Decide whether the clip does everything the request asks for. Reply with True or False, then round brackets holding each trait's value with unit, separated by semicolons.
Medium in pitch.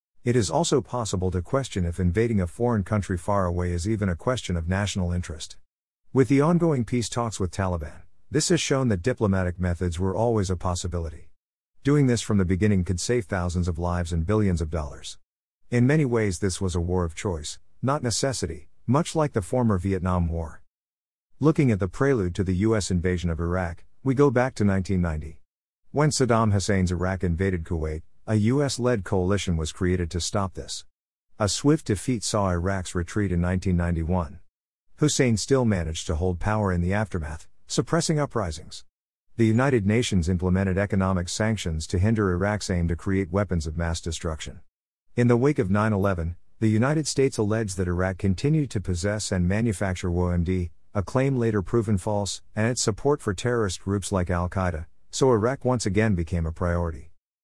False (95 Hz)